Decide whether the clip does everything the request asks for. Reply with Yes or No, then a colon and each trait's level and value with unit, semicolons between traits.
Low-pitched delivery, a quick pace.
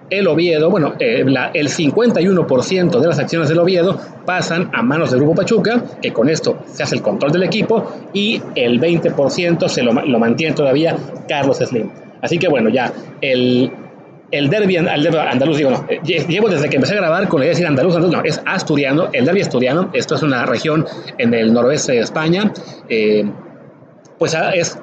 No: medium, 170 Hz; fast, 195 wpm